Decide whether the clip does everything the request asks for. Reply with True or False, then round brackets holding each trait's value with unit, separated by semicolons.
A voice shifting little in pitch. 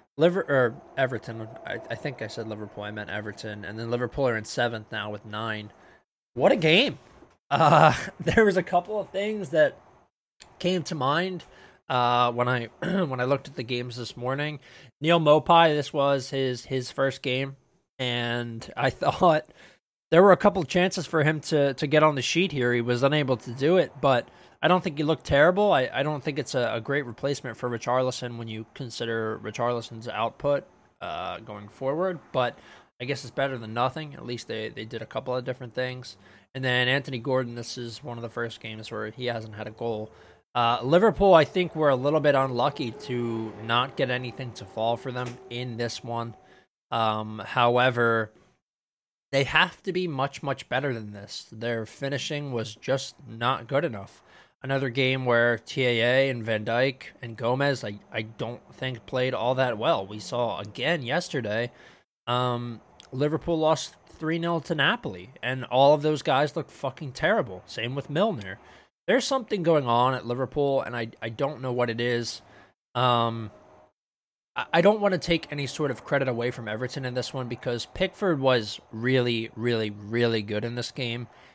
False (3.8 semitones)